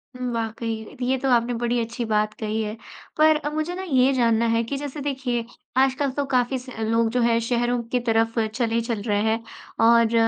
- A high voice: Yes, high, 235 Hz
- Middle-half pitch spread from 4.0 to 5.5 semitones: No, narrow, 2.5 semitones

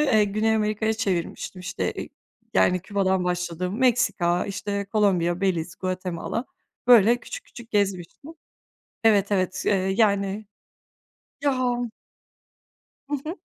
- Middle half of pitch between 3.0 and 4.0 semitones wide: Yes, average, 3.3 semitones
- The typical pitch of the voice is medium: No, high, 200 Hz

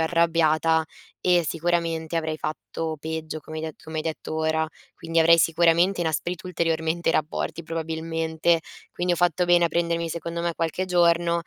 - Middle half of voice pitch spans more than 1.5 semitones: No, narrow, 1.2 semitones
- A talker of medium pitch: Yes, medium, 165 Hz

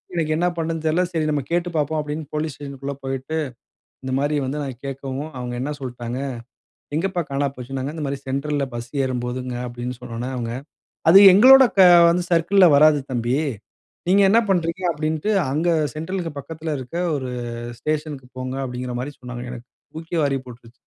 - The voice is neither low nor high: Yes, medium, 145 Hz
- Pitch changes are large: No, average, 4.0 semitones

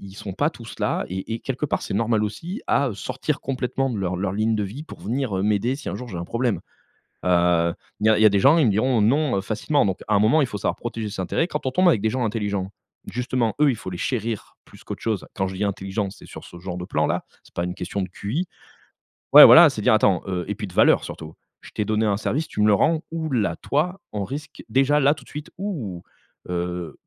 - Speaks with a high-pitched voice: No, low, 110 Hz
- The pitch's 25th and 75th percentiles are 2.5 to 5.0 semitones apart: No, wide, 5.6 semitones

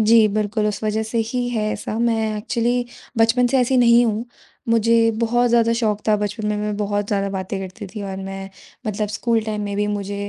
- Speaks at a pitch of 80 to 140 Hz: No, high, 215 Hz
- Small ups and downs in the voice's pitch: Yes, narrow, 2.1 semitones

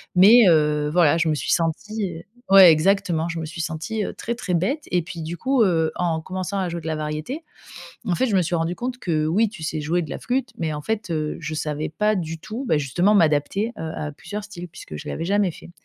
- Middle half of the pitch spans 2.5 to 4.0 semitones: No, average, 4.4 semitones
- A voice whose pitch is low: No, medium, 170 Hz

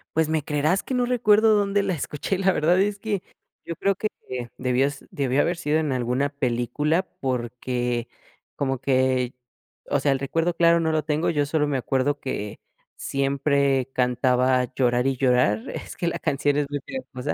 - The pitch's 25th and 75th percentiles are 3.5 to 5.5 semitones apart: Yes, average, 4.4 semitones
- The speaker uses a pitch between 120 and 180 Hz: Yes, medium, 140 Hz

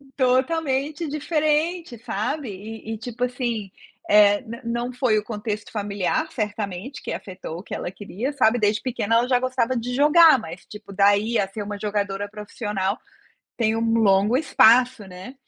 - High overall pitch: Yes, high, 225 Hz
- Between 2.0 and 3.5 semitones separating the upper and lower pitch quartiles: No, average, 3.9 semitones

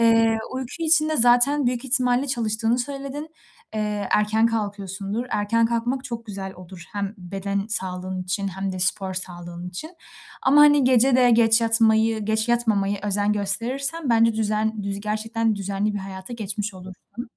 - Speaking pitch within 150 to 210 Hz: No, high, 220 Hz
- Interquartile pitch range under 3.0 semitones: No, average, 3.5 semitones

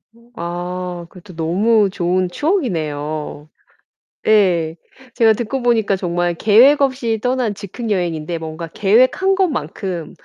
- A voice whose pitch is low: No, high, 190 Hz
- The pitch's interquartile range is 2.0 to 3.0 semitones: No, wide, 5.4 semitones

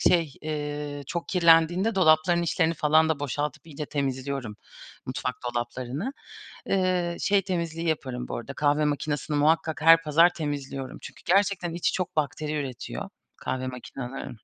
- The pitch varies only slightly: No, average, 3.5 semitones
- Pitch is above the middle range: No, medium, 155 Hz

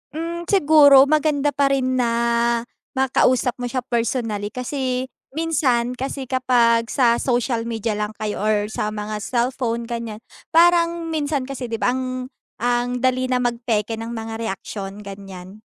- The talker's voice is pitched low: No, high, 245 Hz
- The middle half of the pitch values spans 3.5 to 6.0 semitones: No, average, 3.1 semitones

